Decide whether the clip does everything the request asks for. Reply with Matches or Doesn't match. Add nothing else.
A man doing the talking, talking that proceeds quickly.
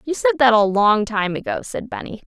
Doesn't match